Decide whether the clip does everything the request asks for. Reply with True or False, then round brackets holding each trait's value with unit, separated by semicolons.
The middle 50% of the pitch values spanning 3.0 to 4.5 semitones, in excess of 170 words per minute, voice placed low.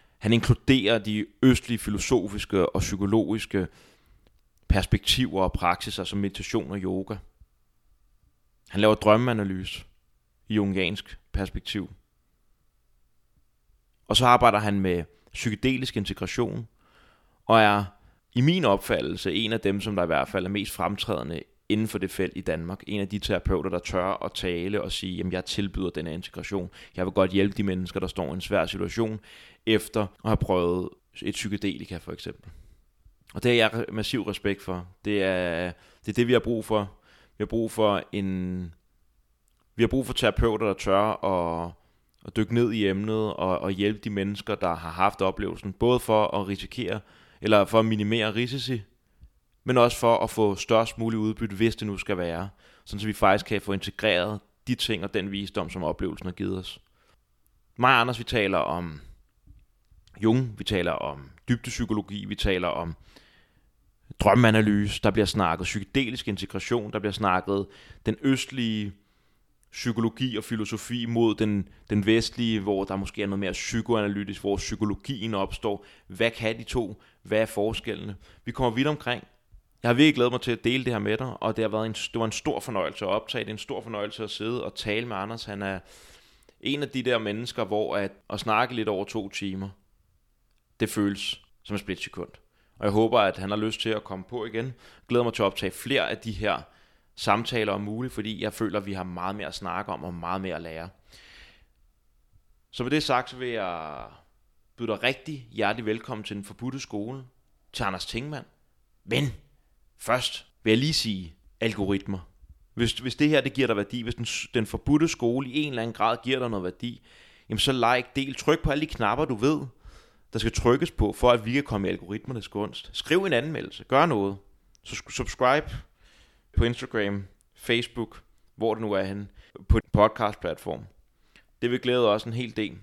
True (3.3 semitones; 185 wpm; 105 Hz)